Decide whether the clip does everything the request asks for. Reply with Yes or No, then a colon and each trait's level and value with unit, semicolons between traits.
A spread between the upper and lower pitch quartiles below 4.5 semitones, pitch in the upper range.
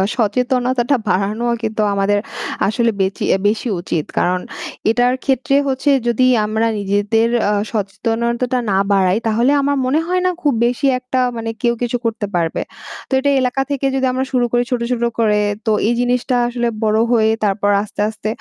Yes: average, 3.1 semitones; high, 235 Hz